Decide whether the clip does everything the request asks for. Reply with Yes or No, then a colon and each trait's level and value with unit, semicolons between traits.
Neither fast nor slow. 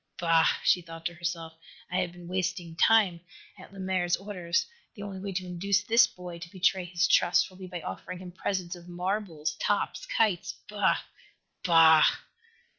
Yes: average, 170 wpm